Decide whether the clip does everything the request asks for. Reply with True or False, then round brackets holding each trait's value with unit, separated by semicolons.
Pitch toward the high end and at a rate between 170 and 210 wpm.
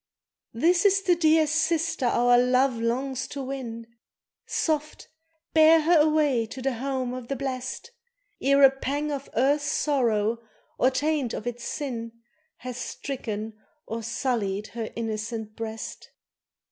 False (260 Hz; 135 wpm)